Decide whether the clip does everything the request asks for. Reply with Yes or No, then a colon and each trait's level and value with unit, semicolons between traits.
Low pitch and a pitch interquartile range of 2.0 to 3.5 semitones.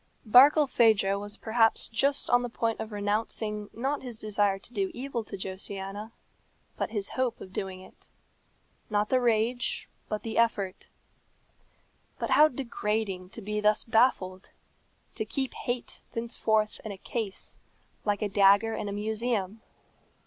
No: high, 215 Hz; average, 2.7 semitones